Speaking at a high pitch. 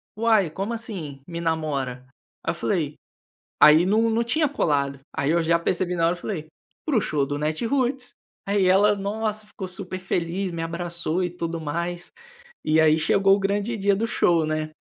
No: medium, 175 Hz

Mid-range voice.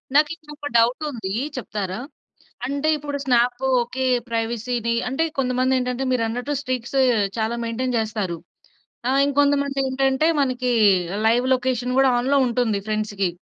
No: very high, 250 Hz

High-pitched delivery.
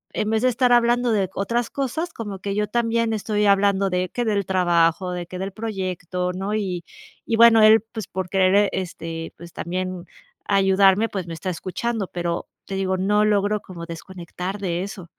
Yes: high, 195 Hz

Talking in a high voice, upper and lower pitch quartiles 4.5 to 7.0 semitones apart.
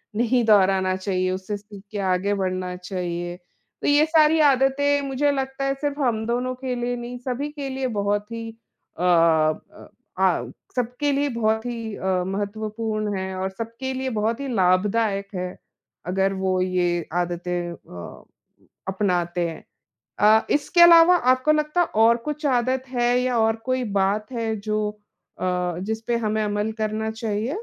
Yes: high, 220 Hz; average, 5.2 semitones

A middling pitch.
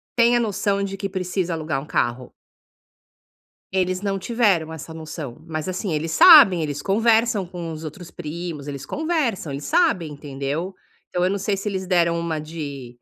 Yes: medium, 175 Hz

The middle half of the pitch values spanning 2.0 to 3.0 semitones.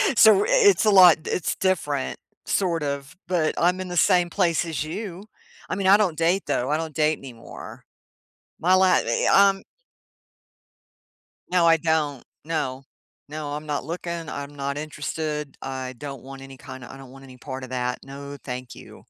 No: average, 4.6 semitones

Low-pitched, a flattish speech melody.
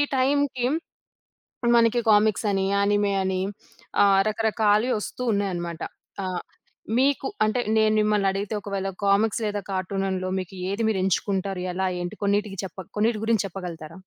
No: high, 200 Hz; narrow, 2.2 semitones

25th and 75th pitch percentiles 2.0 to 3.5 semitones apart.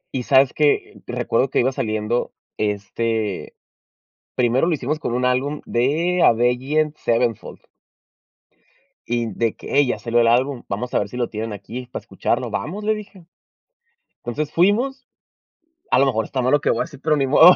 No: average, 4.5 semitones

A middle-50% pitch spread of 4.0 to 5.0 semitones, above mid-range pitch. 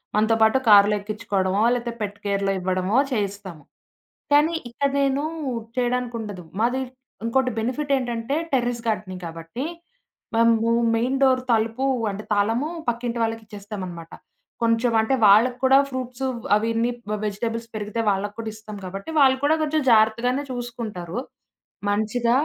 No: average, 3.2 semitones; high, 230 Hz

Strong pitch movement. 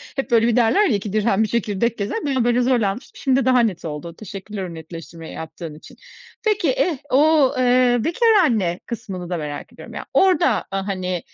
Yes: wide, 5.8 semitones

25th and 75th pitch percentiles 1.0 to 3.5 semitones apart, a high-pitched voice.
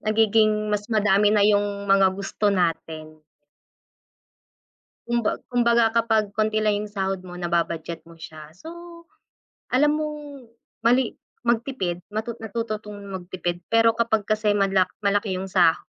Yes: average, 3.0 semitones; high, 205 Hz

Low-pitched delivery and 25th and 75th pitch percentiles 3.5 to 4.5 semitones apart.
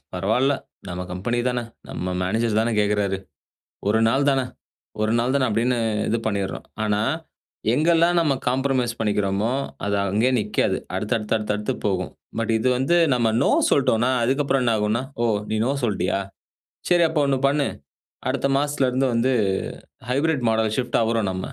Yes: low, 115 Hz; average, 4.1 semitones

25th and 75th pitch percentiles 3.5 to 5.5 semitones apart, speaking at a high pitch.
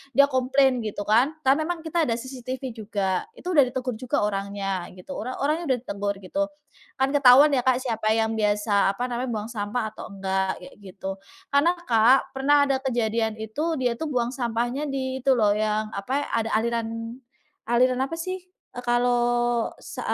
Yes: average, 3.8 semitones; high, 240 Hz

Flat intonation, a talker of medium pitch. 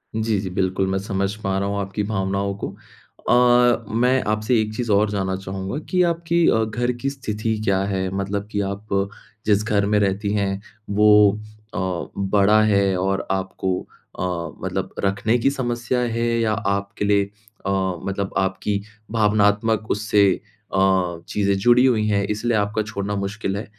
No: narrow, 2.0 semitones; low, 100 Hz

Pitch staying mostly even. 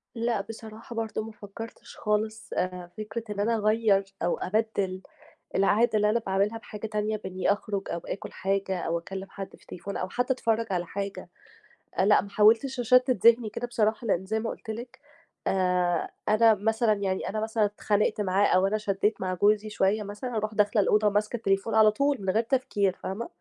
Yes: narrow, 2.3 semitones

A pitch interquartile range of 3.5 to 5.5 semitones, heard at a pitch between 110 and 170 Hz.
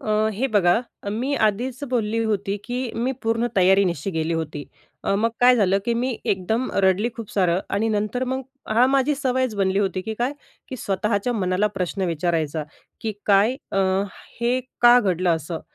No: average, 4.3 semitones; high, 210 Hz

